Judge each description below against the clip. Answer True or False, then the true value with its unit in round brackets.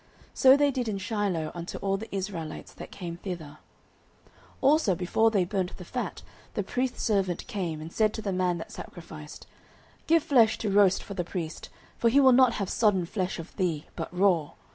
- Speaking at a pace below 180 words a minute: False (195 wpm)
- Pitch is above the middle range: True (195 Hz)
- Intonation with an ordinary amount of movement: True (4.4 semitones)